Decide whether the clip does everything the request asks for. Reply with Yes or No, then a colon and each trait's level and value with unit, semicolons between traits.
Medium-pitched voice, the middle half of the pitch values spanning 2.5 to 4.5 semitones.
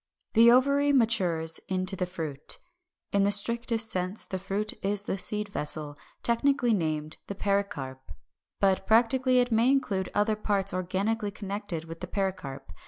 No: high, 200 Hz; average, 3.8 semitones